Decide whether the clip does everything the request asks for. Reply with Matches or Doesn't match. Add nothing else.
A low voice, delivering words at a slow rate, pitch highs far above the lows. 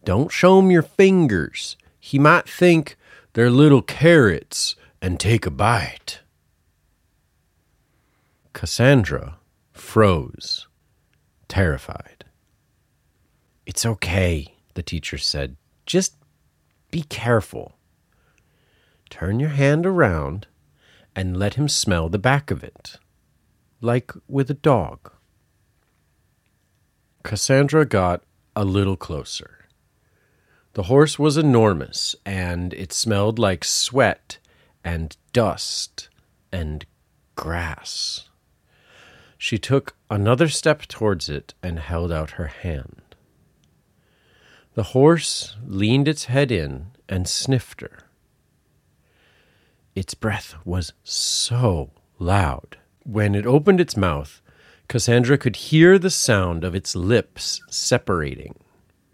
Matches